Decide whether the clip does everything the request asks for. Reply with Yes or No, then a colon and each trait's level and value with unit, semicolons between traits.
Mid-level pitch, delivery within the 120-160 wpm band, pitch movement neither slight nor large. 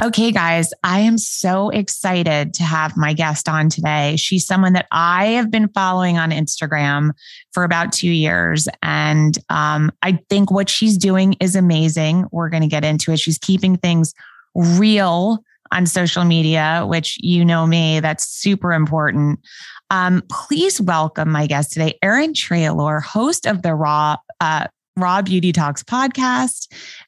Yes: medium, 170 Hz; average, 155 wpm; average, 3.7 semitones